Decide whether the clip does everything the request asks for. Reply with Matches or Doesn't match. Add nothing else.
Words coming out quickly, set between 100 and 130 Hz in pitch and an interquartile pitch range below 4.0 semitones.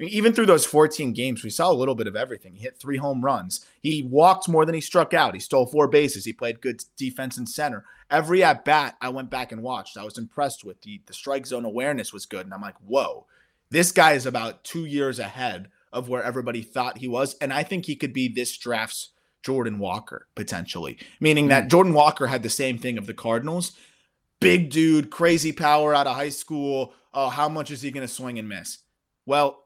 Doesn't match